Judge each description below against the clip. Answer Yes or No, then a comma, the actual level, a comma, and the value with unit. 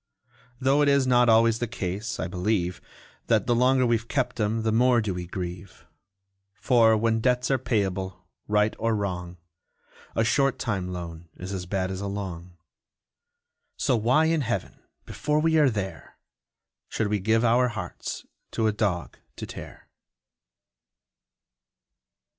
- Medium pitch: No, low, 110 Hz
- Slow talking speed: No, average, 150 wpm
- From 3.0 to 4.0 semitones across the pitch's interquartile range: No, average, 4.6 semitones